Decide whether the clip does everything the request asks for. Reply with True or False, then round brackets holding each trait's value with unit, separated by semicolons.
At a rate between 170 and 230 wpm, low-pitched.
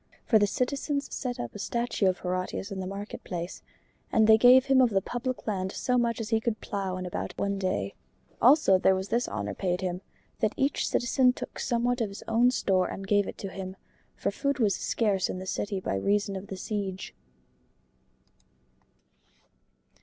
False (190 wpm; 205 Hz)